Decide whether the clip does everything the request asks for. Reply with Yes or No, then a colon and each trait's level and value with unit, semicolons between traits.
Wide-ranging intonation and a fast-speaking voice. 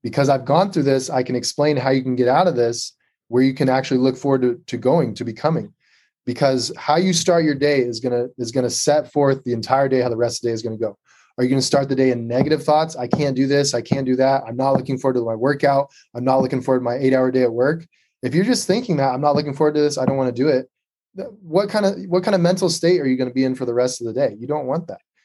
No: average, 3.1 semitones; fast, 295 wpm